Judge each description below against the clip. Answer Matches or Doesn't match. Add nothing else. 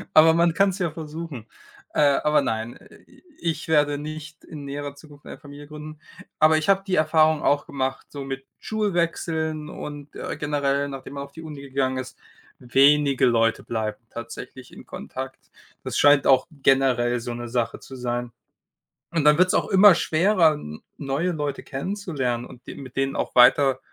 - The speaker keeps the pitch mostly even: Doesn't match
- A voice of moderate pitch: Matches